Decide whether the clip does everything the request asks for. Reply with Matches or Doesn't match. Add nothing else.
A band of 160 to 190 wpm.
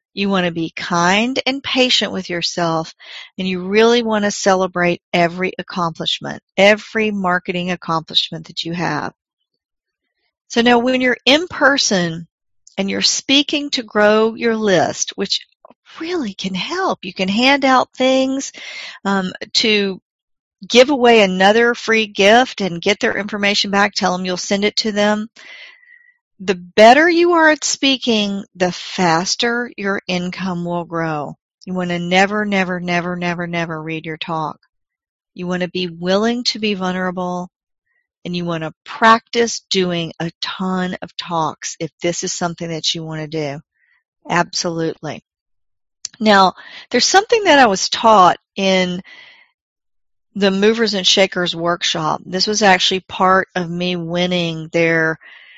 Doesn't match